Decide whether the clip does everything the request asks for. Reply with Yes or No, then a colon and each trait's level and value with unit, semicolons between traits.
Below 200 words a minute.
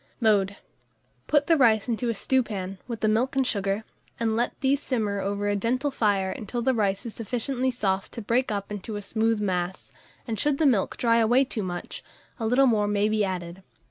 No: fast, 205 wpm